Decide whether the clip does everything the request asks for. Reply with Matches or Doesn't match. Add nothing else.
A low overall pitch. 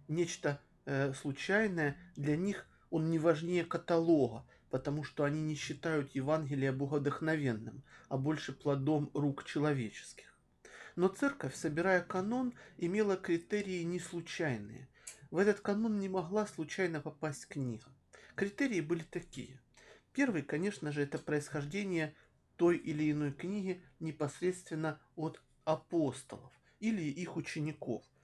Doesn't match